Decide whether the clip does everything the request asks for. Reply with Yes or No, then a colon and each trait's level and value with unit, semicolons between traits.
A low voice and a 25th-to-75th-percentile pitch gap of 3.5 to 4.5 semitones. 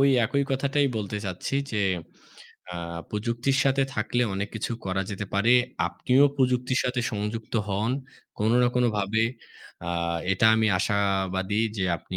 Yes: low, 110 Hz; average, 3.9 semitones